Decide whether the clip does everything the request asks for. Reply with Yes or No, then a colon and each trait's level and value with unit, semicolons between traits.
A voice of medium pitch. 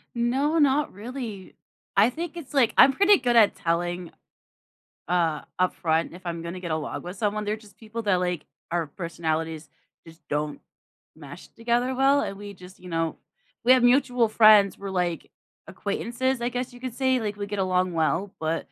No: high, 205 Hz